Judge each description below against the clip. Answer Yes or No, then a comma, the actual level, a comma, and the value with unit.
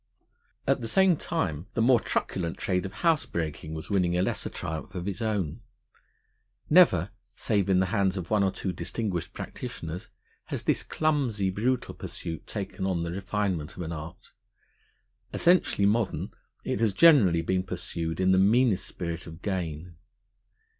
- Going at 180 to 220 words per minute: No, average, 155 wpm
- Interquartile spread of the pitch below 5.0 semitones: Yes, average, 4.3 semitones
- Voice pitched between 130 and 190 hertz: No, very low, 95 Hz